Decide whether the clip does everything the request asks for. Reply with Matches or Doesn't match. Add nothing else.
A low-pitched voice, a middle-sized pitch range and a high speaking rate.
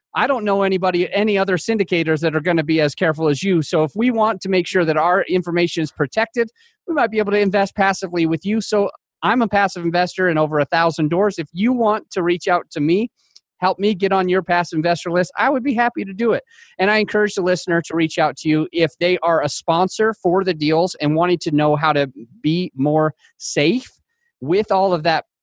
Doesn't match